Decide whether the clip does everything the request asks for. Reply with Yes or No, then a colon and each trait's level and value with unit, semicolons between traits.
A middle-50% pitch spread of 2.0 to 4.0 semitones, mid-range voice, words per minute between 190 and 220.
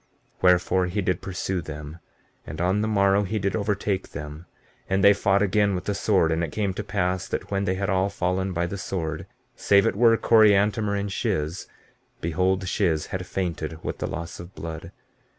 No: average, 2.7 semitones; very low, 95 Hz; average, 195 wpm